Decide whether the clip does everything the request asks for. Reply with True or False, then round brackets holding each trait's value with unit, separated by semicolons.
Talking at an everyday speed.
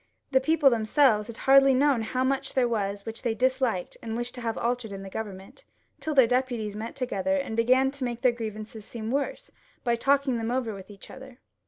False (210 wpm)